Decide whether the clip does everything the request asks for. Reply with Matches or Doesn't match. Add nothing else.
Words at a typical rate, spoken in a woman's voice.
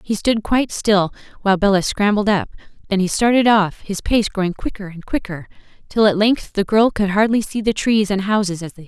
Doesn't match